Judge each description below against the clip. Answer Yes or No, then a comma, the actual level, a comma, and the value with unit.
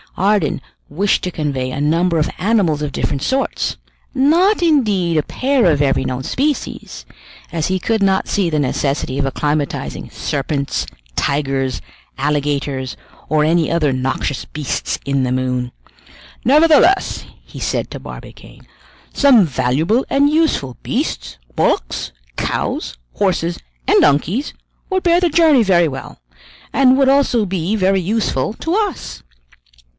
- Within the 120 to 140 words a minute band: Yes, slow, 135 wpm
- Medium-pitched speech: Yes, medium, 170 Hz